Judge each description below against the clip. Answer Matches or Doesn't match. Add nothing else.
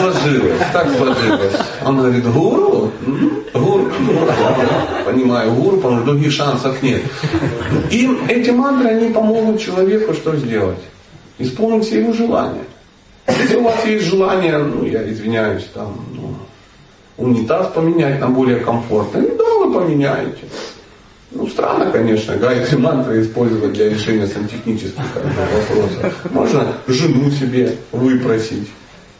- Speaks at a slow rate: Doesn't match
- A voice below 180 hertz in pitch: Matches